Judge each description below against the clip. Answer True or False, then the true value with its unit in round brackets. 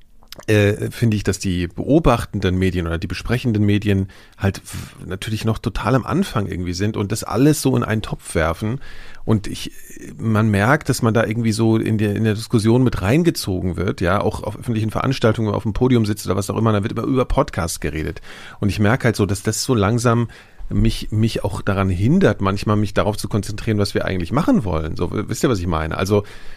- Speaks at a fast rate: True (215 wpm)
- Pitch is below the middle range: True (105 Hz)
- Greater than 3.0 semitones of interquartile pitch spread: False (2.7 semitones)